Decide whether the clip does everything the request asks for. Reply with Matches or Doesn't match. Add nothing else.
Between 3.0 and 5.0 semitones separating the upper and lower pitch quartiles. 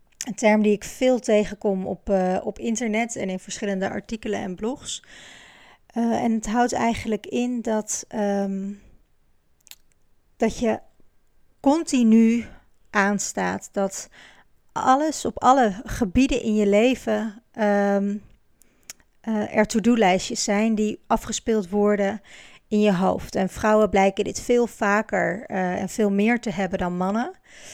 Doesn't match